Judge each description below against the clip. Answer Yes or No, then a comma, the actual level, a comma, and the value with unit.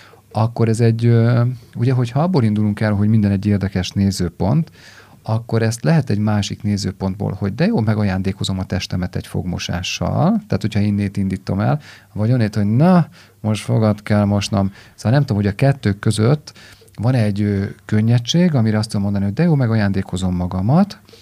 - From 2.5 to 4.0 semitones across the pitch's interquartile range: Yes, average, 2.9 semitones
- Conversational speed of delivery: No, fast, 170 wpm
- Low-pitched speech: Yes, low, 105 Hz